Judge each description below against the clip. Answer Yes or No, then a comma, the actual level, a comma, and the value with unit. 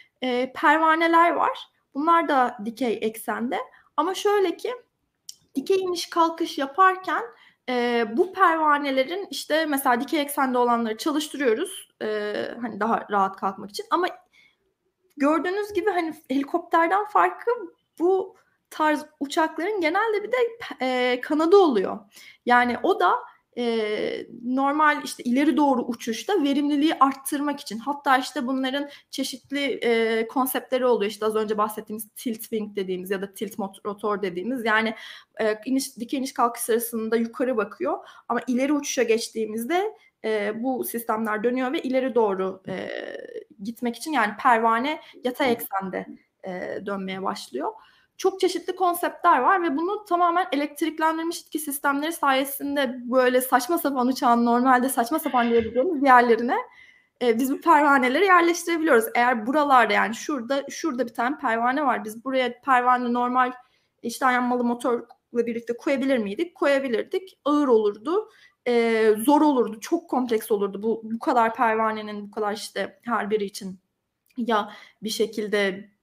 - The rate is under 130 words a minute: No, average, 135 wpm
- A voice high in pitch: Yes, very high, 260 Hz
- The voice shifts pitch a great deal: Yes, wide, 5.9 semitones